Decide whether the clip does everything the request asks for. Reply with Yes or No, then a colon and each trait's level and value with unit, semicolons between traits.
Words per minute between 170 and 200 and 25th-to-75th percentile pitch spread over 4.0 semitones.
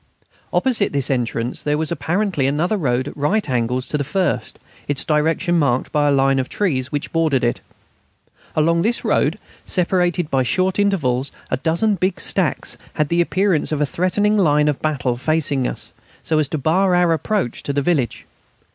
Yes: average, 180 wpm; average, 4.6 semitones